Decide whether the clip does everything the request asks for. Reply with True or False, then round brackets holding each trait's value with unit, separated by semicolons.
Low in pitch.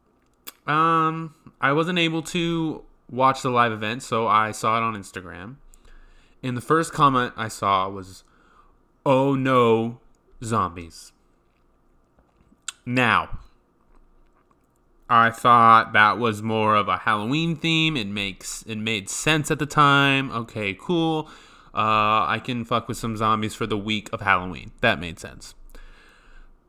True (115 Hz)